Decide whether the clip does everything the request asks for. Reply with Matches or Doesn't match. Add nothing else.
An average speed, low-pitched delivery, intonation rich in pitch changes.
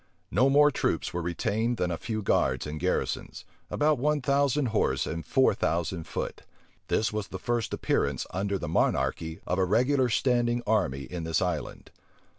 Matches